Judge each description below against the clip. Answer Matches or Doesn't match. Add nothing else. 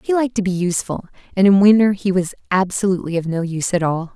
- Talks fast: Matches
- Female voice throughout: Matches